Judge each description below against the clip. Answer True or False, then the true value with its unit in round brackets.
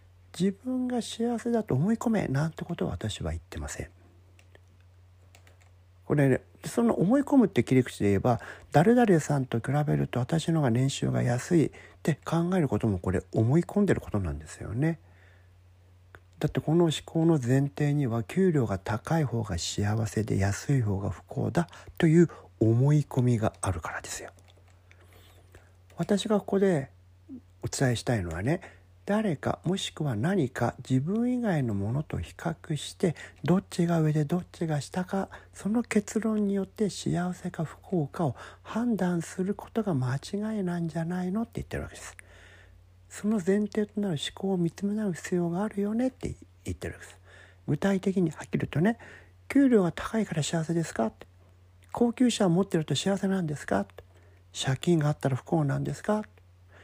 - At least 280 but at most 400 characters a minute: True (290 characters per minute)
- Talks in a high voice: False (140 Hz)